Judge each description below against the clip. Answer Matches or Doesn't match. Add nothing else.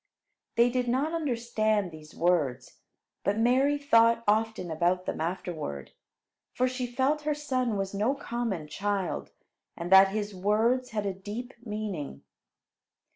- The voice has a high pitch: Matches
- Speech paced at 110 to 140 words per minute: Matches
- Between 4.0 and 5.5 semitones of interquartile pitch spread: Matches